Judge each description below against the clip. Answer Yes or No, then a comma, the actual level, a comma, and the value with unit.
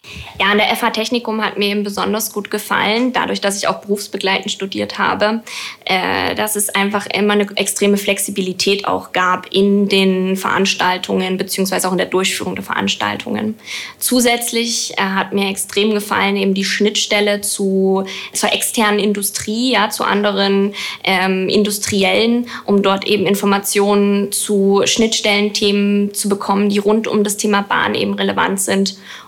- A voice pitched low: No, high, 200 Hz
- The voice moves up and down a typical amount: No, narrow, 1.3 semitones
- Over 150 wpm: No, average, 145 wpm